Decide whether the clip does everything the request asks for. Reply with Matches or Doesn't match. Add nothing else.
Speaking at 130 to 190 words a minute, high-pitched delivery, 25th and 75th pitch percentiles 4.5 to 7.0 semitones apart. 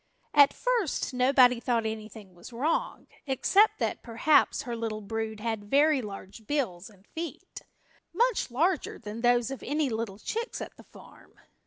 Matches